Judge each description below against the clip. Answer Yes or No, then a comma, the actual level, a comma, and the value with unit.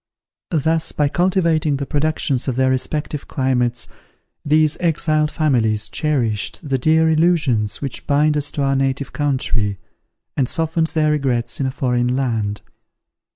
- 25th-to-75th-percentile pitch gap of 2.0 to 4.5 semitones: Yes, average, 3.6 semitones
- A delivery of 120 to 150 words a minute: Yes, average, 140 wpm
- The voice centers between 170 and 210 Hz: No, medium, 140 Hz